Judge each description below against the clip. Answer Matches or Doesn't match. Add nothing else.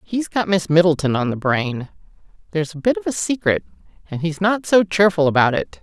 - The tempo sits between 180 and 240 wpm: Matches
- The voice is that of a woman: Matches